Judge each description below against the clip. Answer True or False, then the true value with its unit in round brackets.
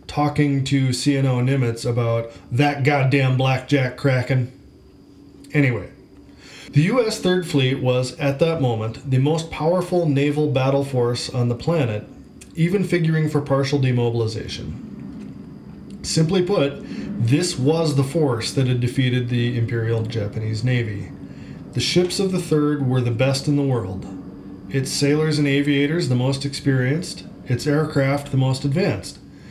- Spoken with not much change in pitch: False (3.3 semitones)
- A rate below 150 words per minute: True (140 wpm)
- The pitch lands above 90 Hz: True (135 Hz)